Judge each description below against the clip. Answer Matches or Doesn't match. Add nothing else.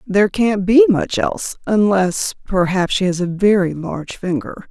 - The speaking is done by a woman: Matches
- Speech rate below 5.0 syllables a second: Matches